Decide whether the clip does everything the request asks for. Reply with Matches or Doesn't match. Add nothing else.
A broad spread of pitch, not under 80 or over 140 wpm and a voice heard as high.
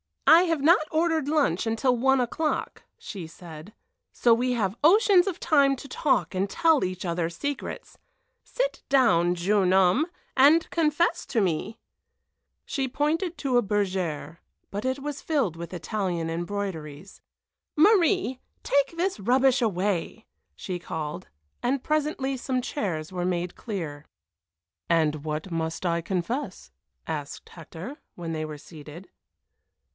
Matches